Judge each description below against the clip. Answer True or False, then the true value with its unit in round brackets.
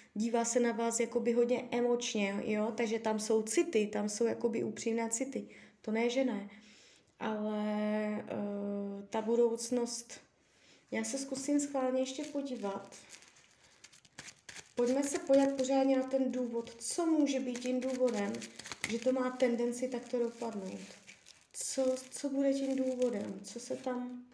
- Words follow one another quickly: False (140 wpm)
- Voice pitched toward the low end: False (240 Hz)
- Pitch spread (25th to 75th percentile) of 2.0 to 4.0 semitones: True (2.8 semitones)